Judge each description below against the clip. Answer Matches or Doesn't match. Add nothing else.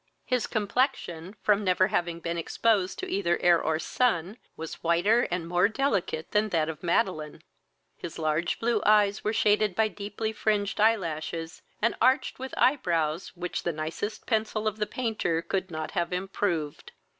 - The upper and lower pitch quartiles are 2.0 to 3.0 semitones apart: Doesn't match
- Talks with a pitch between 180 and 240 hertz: Matches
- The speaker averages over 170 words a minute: Doesn't match